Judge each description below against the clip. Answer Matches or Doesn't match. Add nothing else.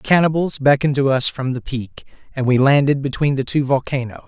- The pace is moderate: Doesn't match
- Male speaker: Matches